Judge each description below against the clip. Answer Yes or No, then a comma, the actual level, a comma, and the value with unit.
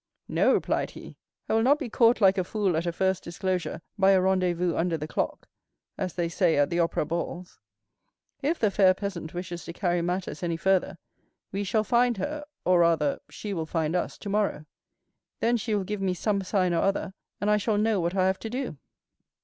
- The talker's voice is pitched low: No, medium, 185 Hz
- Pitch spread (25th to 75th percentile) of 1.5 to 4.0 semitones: Yes, average, 3.3 semitones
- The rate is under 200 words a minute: No, fast, 205 wpm